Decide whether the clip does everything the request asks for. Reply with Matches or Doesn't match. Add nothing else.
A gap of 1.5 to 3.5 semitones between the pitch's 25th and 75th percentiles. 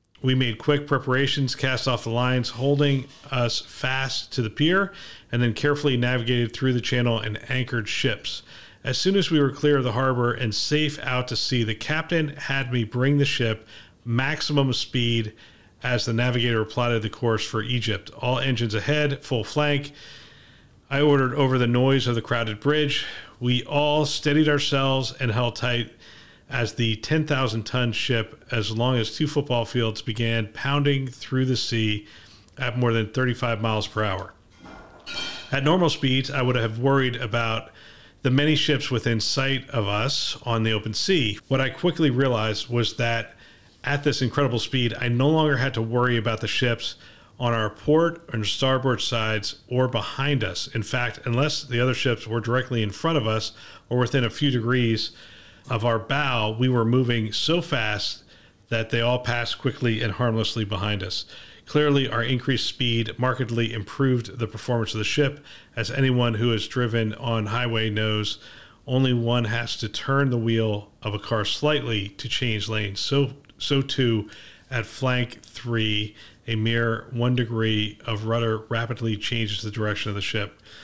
Matches